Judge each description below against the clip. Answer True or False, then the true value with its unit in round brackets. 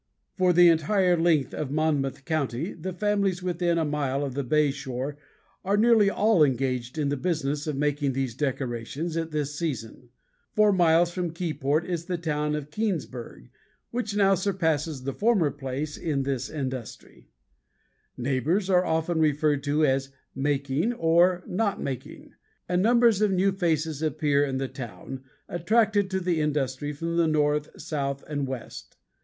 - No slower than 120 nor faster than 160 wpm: True (155 wpm)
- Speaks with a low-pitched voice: False (155 Hz)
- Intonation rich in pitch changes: False (4.3 semitones)